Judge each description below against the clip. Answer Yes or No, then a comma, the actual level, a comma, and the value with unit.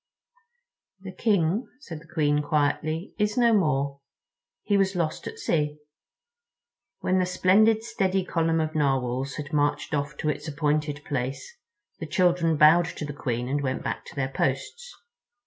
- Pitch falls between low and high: Yes, medium, 155 Hz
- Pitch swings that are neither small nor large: Yes, average, 4.1 semitones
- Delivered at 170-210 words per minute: No, average, 155 wpm